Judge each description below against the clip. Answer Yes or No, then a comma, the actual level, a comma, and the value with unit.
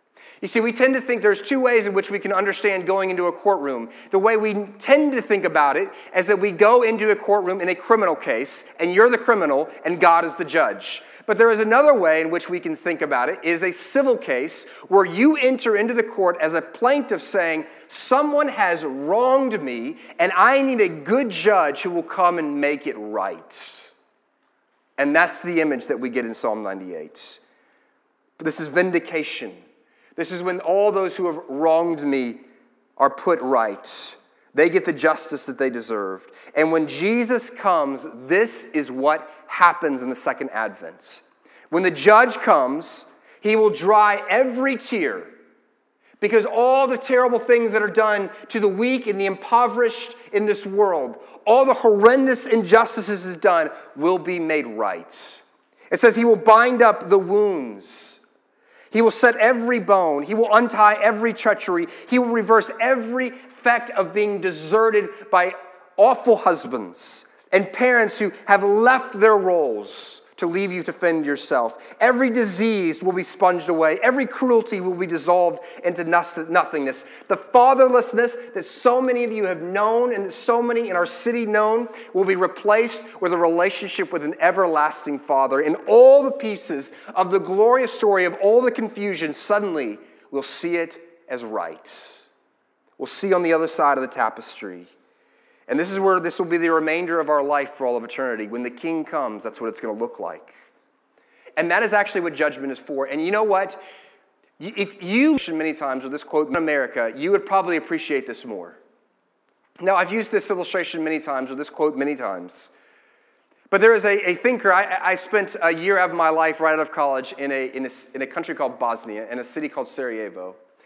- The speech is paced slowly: No, average, 185 wpm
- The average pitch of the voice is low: No, high, 195 Hz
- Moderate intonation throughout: No, wide, 6.1 semitones